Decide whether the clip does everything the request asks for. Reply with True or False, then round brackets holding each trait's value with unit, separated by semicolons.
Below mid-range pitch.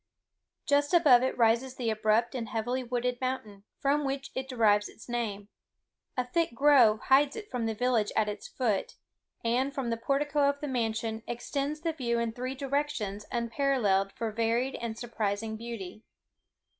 False (240 Hz)